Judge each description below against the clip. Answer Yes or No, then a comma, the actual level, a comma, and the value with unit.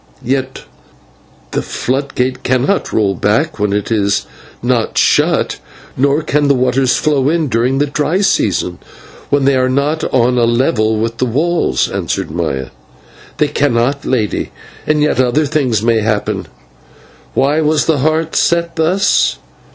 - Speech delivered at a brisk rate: No, average, 150 wpm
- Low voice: Yes, low, 130 Hz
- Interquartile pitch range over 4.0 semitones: Yes, average, 4.5 semitones